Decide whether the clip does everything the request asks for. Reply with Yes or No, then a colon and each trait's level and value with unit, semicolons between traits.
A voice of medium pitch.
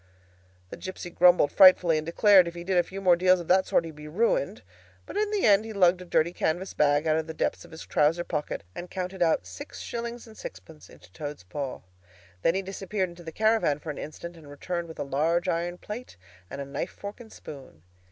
Yes: medium, 175 Hz